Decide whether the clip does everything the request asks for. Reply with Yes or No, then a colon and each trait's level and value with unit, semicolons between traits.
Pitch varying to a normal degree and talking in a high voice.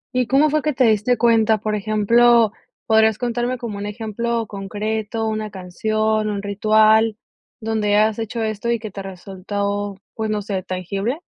No: narrow, 2.0 semitones; high, 215 Hz